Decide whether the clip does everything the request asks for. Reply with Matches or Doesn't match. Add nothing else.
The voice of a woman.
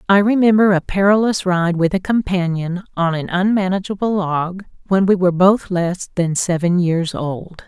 Matches